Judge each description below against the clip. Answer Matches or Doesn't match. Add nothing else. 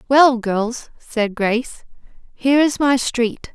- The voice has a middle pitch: Doesn't match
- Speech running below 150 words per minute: Matches